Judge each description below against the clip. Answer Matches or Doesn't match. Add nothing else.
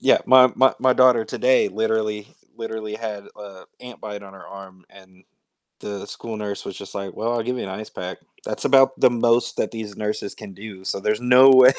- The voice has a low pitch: Matches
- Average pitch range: Matches